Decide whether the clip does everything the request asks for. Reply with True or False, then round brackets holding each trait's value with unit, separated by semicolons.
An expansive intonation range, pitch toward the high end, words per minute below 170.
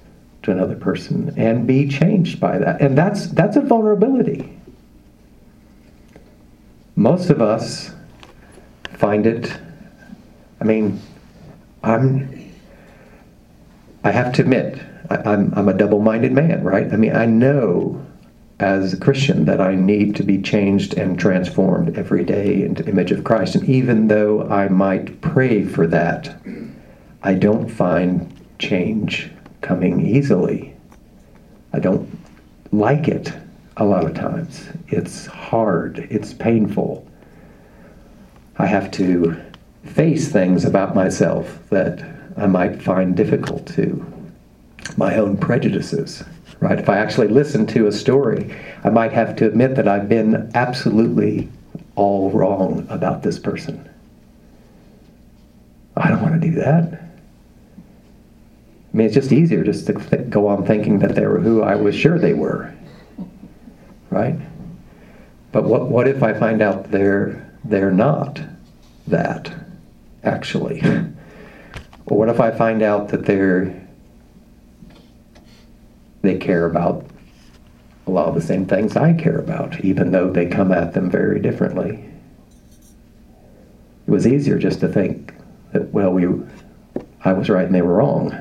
False (6.5 semitones; 105 Hz; 135 wpm)